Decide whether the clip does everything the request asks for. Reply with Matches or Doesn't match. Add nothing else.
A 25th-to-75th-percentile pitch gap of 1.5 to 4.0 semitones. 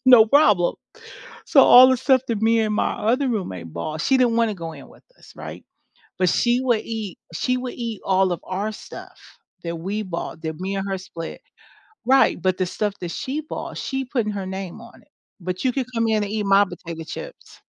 Doesn't match